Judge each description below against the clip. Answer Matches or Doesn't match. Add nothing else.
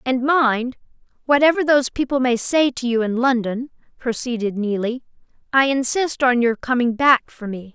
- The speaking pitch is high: Matches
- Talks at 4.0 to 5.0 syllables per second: Matches